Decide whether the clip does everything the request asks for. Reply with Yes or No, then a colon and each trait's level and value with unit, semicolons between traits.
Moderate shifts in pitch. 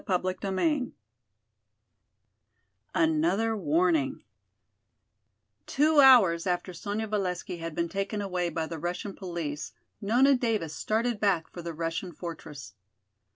Yes: average, 4.3 semitones